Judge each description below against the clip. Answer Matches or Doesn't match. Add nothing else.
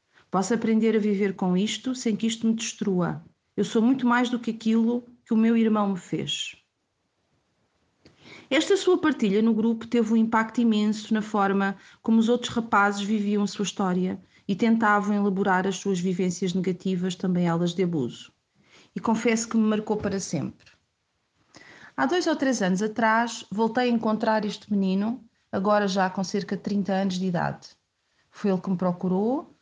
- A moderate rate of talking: Matches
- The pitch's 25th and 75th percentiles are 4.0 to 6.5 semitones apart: Doesn't match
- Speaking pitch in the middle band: Doesn't match